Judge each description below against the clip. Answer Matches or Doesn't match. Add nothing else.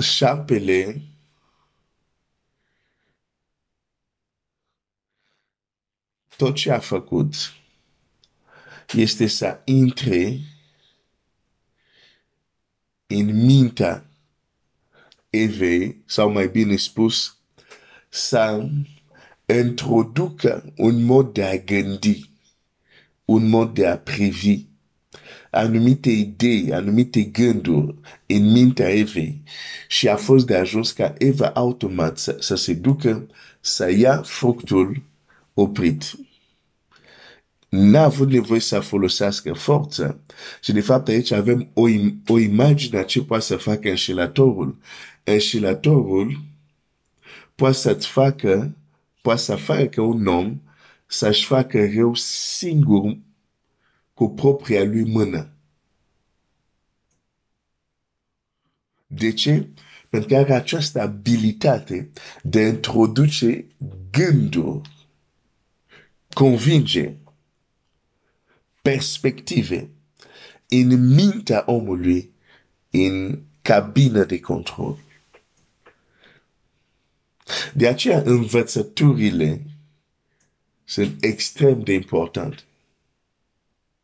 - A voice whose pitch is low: Matches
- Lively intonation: Matches